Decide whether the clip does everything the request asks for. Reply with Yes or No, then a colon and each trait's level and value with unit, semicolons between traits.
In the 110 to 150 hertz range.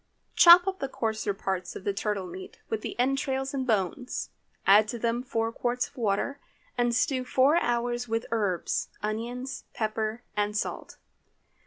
No: high, 230 Hz